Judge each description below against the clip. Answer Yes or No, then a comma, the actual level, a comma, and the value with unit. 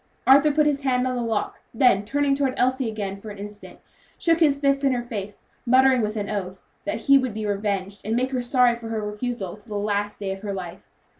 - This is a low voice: No, high, 230 Hz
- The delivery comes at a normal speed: No, fast, 235 wpm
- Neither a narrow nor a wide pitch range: Yes, average, 4.3 semitones